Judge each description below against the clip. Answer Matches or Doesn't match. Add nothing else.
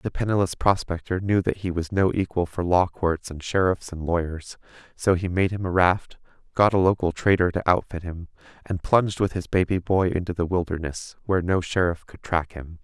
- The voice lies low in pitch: Matches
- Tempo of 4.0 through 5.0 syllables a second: Doesn't match